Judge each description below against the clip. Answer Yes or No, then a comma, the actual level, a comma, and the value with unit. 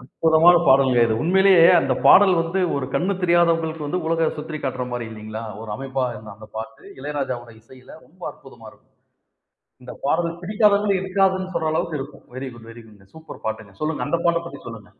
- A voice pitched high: No, medium, 155 Hz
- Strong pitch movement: Yes, wide, 5.7 semitones